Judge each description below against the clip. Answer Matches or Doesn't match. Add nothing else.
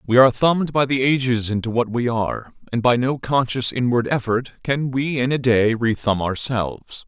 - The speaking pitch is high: Doesn't match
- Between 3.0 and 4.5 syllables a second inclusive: Doesn't match